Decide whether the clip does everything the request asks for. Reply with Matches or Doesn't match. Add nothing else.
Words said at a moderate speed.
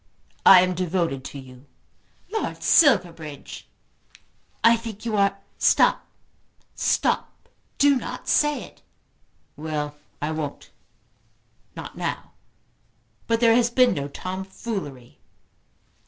Doesn't match